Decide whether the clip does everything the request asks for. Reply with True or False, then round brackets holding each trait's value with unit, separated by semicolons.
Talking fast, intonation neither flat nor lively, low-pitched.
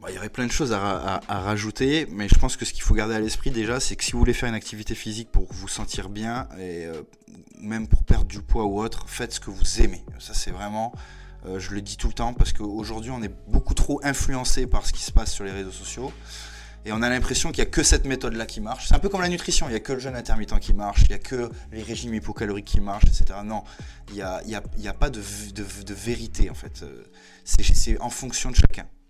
True (270 wpm; 3.5 semitones; 105 Hz)